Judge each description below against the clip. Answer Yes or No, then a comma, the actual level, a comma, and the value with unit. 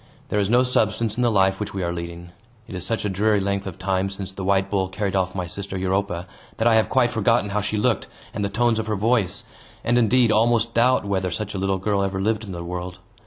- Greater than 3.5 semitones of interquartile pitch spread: No, average, 2.7 semitones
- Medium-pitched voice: No, low, 100 Hz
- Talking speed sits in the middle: No, fast, 255 wpm